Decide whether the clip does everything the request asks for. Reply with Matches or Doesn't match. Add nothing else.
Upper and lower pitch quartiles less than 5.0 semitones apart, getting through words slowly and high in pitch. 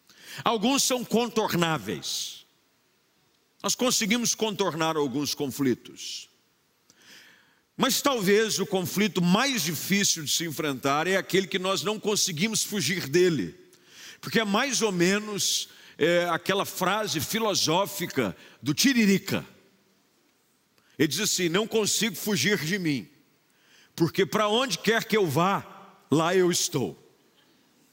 Matches